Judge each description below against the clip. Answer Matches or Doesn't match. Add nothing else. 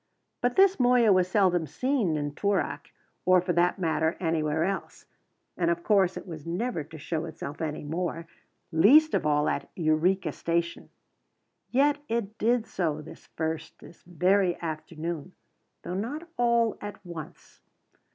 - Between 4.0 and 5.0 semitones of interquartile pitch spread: Matches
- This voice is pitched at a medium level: Matches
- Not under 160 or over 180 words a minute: Doesn't match